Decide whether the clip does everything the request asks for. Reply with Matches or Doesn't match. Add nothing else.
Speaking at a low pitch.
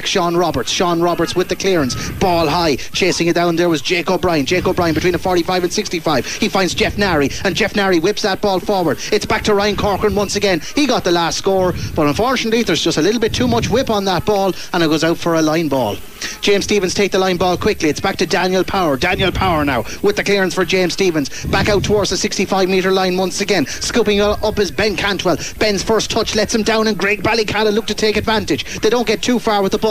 Doesn't match